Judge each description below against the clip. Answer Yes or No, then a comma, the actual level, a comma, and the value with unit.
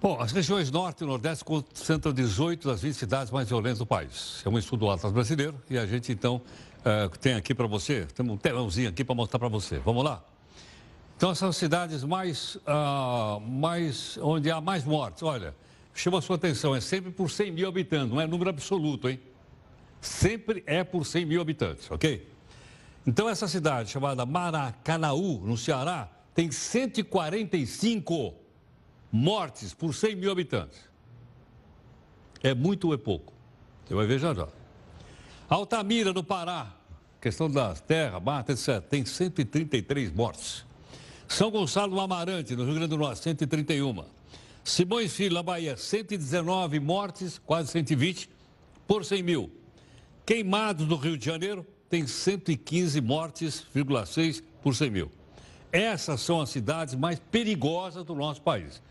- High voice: No, medium, 155 Hz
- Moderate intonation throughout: No, wide, 5.8 semitones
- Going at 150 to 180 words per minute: Yes, average, 155 wpm